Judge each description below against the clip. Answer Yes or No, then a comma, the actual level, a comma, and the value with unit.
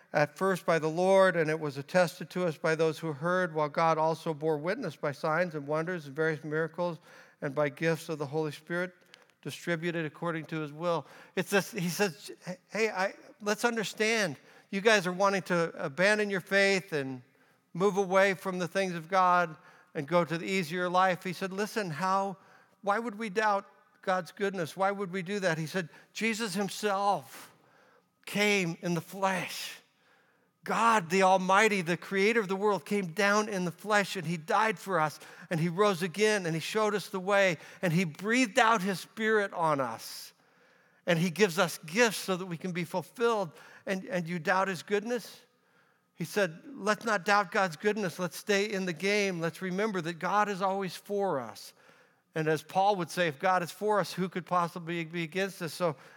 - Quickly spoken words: No, average, 195 wpm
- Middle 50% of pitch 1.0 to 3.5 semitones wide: Yes, average, 3.1 semitones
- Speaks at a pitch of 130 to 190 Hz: Yes, medium, 185 Hz